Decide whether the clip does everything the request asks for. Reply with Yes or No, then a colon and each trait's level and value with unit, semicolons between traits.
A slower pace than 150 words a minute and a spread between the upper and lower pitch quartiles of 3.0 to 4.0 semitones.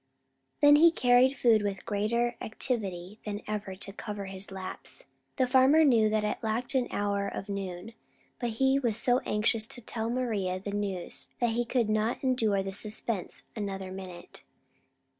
No: average, 165 wpm; average, 3.5 semitones